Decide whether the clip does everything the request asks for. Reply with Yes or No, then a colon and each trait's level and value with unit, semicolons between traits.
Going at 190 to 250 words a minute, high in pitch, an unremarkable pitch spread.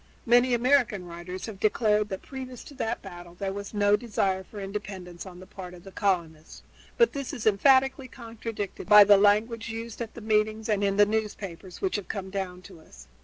Yes: average, 200 wpm; high, 205 Hz; average, 3.2 semitones